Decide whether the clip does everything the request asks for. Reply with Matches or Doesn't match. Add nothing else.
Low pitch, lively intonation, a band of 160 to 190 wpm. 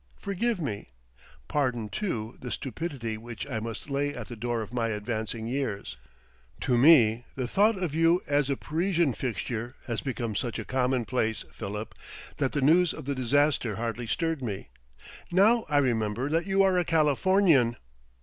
Matches